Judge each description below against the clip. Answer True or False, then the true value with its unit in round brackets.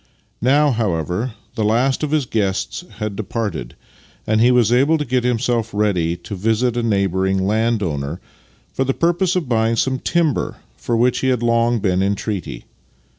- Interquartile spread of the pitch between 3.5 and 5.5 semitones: True (4.2 semitones)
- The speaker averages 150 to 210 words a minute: True (170 wpm)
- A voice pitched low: True (115 Hz)